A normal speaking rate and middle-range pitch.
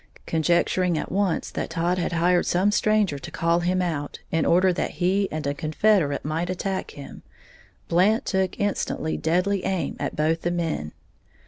Yes: average, 165 wpm; medium, 175 Hz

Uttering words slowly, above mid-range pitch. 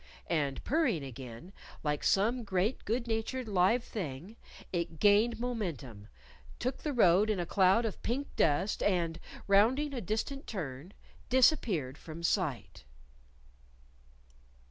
Yes: slow, 120 wpm; high, 195 Hz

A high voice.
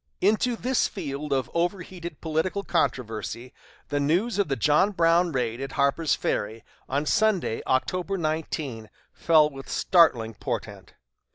No: medium, 155 Hz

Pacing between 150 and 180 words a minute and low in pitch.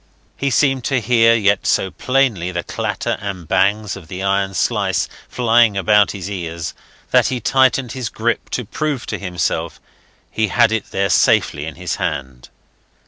Yes: average, 165 wpm; low, 105 Hz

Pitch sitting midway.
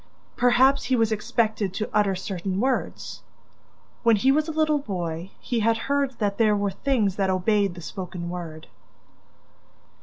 No: high, 210 Hz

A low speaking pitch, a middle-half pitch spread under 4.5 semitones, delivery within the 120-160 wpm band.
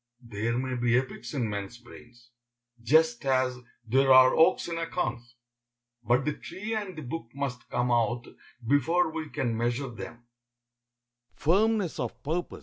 Yes: low, 125 Hz; average, 4.1 semitones; slow, 135 wpm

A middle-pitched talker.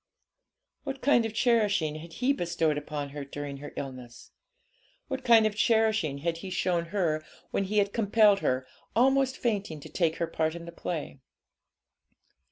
Yes: medium, 175 Hz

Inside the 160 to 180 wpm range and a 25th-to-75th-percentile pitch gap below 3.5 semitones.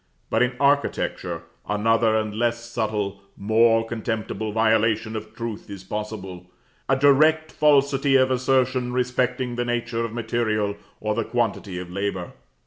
No: average, 140 wpm; average, 2.7 semitones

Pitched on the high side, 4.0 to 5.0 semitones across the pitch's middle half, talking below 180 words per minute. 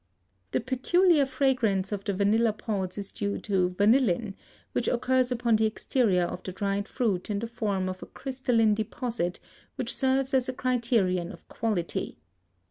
Yes: high, 220 Hz; average, 4.3 semitones; average, 160 wpm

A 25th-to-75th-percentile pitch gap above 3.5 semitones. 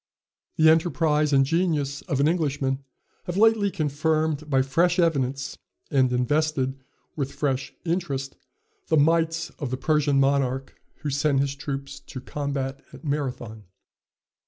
No: average, 2.8 semitones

